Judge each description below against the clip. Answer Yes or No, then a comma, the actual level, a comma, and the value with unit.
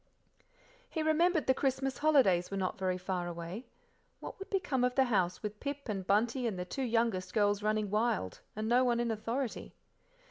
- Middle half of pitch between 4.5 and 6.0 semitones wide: Yes, average, 5.3 semitones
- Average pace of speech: Yes, average, 185 wpm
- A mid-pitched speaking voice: No, high, 225 Hz